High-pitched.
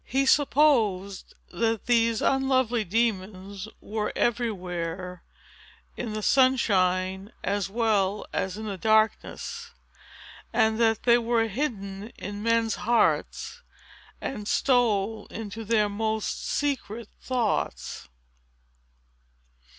Yes: high, 220 Hz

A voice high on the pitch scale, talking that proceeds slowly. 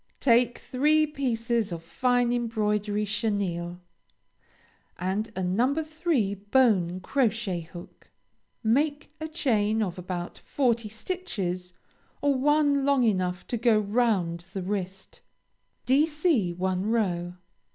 Yes: high, 220 Hz; slow, 110 wpm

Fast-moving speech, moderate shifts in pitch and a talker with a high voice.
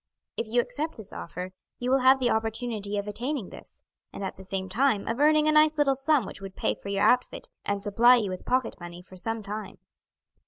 Yes: fast, 225 wpm; average, 4.8 semitones; high, 225 Hz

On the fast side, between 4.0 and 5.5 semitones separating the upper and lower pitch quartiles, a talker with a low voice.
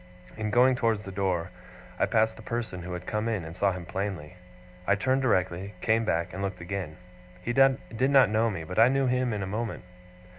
Yes: fast, 215 wpm; average, 4.3 semitones; low, 105 Hz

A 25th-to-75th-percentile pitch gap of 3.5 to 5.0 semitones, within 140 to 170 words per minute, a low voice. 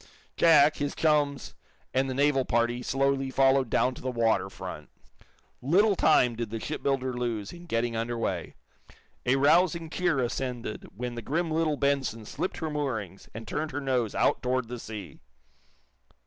Yes: average, 3.8 semitones; average, 160 wpm; low, 130 Hz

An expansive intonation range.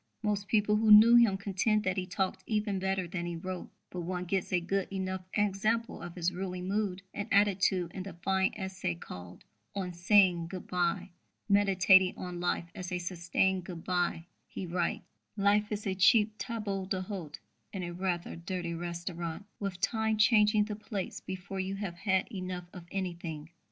No: narrow, 2.4 semitones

